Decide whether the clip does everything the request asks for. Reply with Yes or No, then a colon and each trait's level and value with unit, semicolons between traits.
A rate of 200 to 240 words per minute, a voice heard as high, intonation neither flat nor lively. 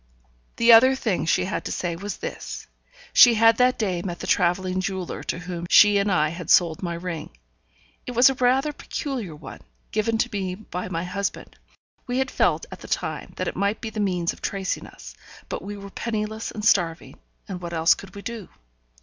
Yes: fast, 205 wpm; high, 195 Hz; average, 4.3 semitones